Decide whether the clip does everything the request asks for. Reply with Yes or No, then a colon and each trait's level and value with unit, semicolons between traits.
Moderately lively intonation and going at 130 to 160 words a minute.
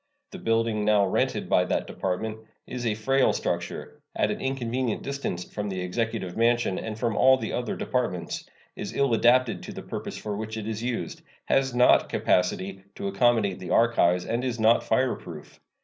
No: average, 3.6 semitones; average, 175 wpm